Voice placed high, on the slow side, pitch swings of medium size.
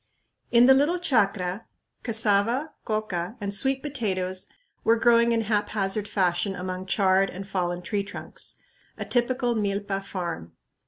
Yes: high, 205 Hz; slow, 130 wpm; average, 3.7 semitones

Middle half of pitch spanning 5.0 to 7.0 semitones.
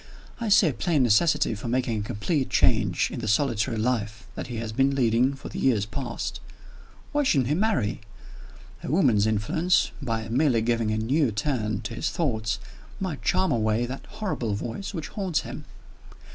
Yes: average, 5.3 semitones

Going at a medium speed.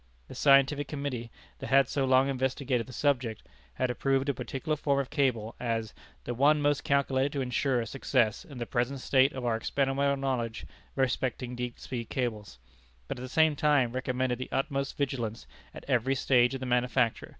Yes: average, 180 wpm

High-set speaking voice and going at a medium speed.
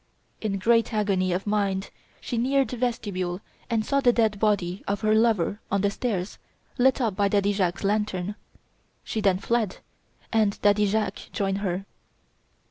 Yes: high, 205 Hz; average, 160 wpm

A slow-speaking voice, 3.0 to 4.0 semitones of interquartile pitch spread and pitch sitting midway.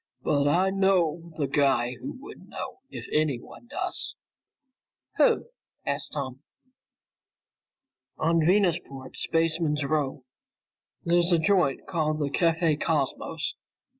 Yes: slow, 110 wpm; average, 3.3 semitones; medium, 155 Hz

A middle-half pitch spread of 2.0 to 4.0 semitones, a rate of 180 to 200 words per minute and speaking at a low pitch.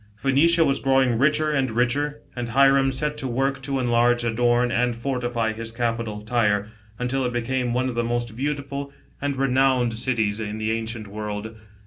No: average, 2.9 semitones; average, 170 wpm; low, 120 Hz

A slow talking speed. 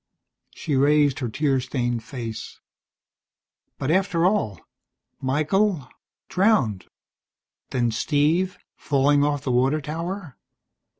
Yes: slow, 100 wpm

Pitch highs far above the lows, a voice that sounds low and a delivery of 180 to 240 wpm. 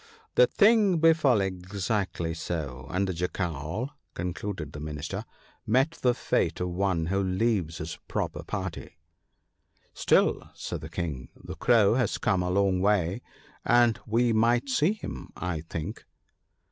No: wide, 6.0 semitones; very low, 95 Hz; average, 160 wpm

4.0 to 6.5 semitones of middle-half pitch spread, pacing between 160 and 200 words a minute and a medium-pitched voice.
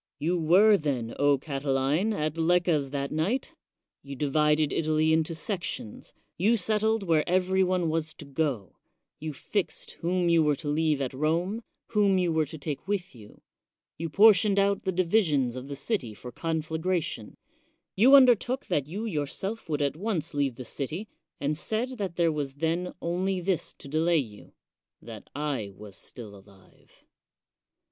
Yes: average, 4.8 semitones; average, 165 wpm; medium, 160 Hz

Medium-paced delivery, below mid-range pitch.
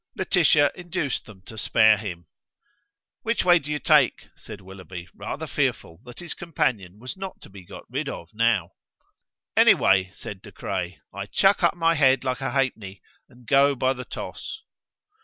Yes: average, 175 wpm; low, 120 Hz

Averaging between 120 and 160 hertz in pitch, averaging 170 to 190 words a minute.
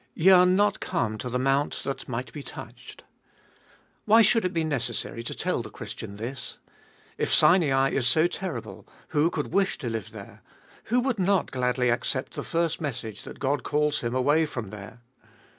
Yes: medium, 140 Hz; average, 180 wpm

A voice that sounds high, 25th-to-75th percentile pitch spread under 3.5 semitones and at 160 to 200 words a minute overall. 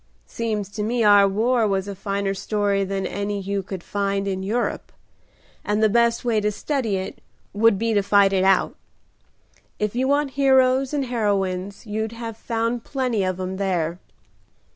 Yes: high, 205 Hz; average, 2.9 semitones; average, 170 wpm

